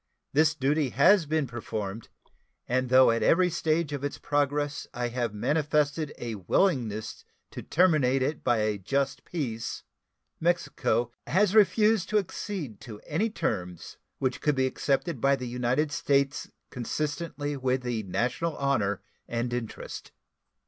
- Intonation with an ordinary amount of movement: Yes, average, 4.4 semitones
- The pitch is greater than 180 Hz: No, medium, 140 Hz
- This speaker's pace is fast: No, average, 140 wpm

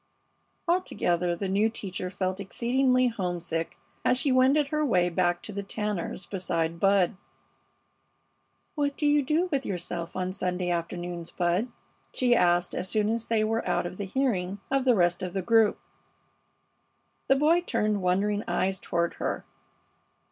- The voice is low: No, high, 200 Hz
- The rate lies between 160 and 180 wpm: No, average, 150 wpm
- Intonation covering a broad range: Yes, wide, 5.8 semitones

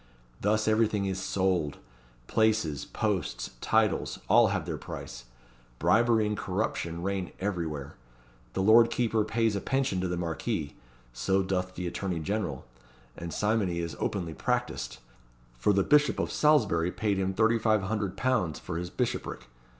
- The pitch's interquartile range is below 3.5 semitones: No, average, 4.1 semitones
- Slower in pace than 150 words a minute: Yes, average, 140 wpm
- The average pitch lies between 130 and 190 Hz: No, very low, 95 Hz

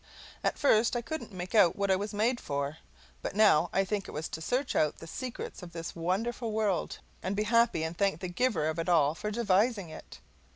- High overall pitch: Yes, high, 195 Hz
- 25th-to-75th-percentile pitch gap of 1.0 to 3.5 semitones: No, average, 5.1 semitones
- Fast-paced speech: Yes, fast, 220 wpm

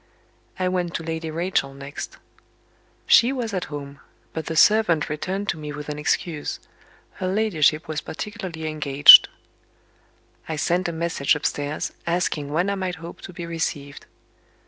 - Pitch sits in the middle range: Yes, medium, 160 Hz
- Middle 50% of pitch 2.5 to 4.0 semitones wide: Yes, average, 3.5 semitones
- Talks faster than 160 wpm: No, average, 150 wpm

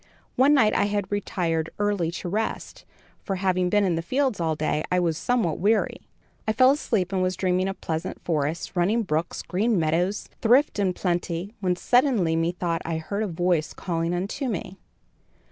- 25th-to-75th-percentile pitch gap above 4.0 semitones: No, average, 3.6 semitones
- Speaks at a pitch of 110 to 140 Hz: No, medium, 185 Hz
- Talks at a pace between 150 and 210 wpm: Yes, average, 180 wpm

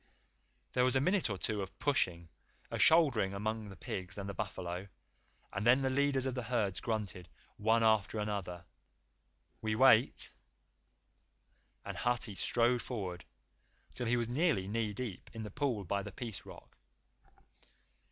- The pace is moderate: Yes, average, 150 wpm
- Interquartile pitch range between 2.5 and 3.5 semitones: No, average, 4.1 semitones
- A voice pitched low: Yes, low, 110 Hz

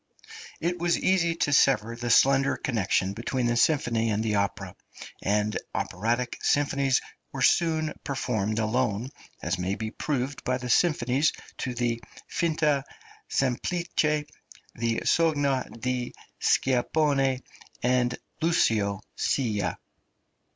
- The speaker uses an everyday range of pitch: Yes, average, 4.3 semitones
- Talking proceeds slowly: Yes, slow, 115 wpm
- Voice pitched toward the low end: Yes, low, 125 Hz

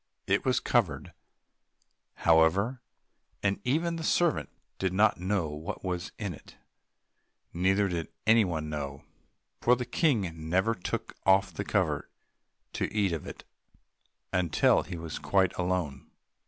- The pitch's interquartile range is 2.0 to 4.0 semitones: No, average, 4.4 semitones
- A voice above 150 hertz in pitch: No, very low, 95 Hz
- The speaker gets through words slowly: Yes, slow, 130 wpm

